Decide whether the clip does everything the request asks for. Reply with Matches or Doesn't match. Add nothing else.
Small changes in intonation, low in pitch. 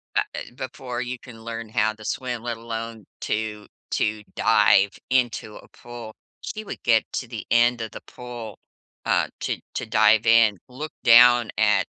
Matches